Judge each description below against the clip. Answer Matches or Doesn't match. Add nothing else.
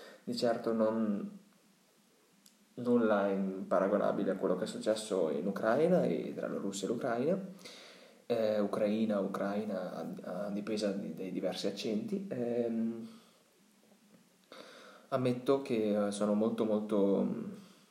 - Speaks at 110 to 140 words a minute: Matches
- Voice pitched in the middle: Doesn't match